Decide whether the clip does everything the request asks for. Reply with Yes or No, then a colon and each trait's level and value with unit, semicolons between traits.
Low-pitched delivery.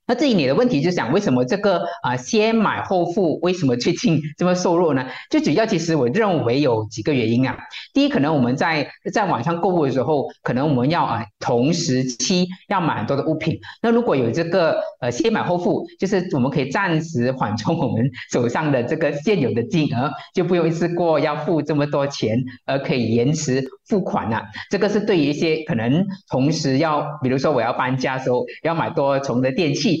No: medium, 155 Hz